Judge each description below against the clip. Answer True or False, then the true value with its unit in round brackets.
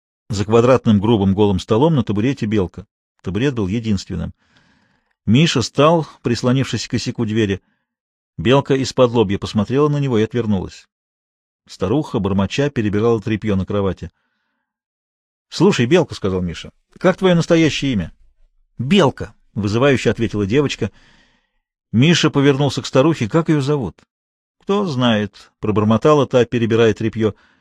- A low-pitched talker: True (115 Hz)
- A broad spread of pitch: True (5.7 semitones)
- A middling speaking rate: True (120 wpm)